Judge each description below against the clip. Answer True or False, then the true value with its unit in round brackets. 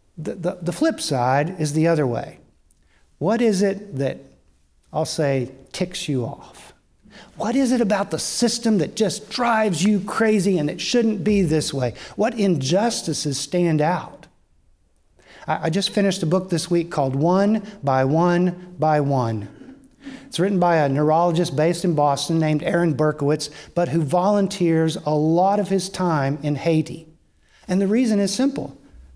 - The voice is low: False (170 Hz)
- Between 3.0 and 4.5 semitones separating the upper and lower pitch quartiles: False (5.3 semitones)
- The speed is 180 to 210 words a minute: False (165 wpm)